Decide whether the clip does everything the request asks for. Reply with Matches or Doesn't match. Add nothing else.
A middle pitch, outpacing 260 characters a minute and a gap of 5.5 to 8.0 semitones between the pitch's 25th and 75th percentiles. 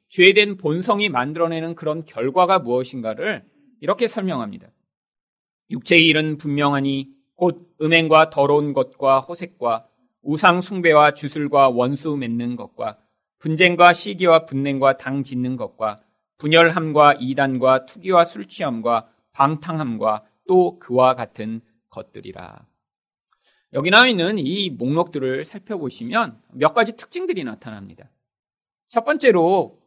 Doesn't match